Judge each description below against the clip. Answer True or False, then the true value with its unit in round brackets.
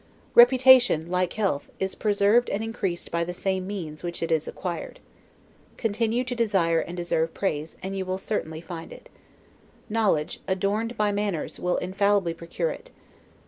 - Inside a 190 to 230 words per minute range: False (160 wpm)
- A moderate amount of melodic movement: True (4.2 semitones)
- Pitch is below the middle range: False (190 Hz)